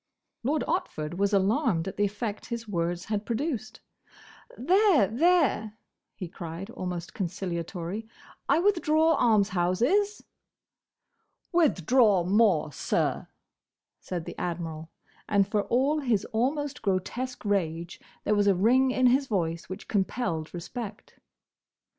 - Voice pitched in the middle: No, high, 205 Hz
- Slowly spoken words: Yes, slow, 115 wpm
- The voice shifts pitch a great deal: Yes, wide, 6.3 semitones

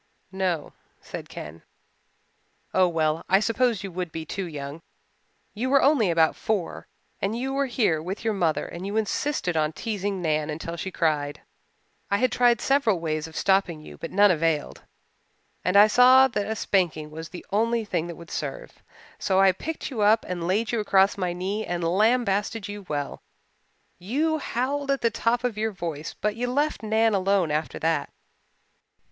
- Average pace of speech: Yes, average, 180 wpm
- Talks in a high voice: Yes, high, 195 Hz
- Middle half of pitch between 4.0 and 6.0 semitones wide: Yes, wide, 5.4 semitones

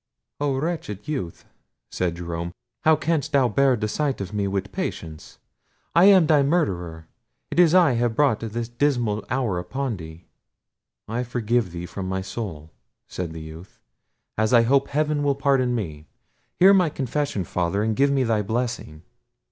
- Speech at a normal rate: Yes, average, 165 wpm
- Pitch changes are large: Yes, wide, 7.2 semitones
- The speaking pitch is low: Yes, low, 115 Hz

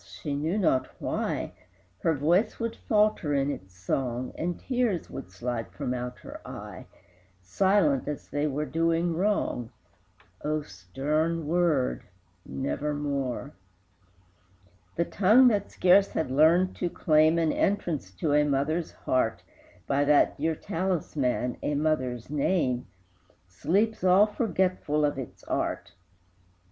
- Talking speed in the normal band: No, slow, 125 wpm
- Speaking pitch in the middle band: Yes, medium, 150 Hz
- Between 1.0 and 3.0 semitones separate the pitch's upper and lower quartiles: No, average, 4.8 semitones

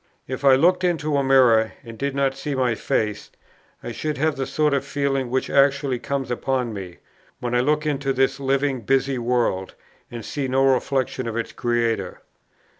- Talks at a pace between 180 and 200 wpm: Yes, average, 185 wpm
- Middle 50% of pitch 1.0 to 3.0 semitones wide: Yes, narrow, 2.5 semitones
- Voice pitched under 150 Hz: Yes, low, 135 Hz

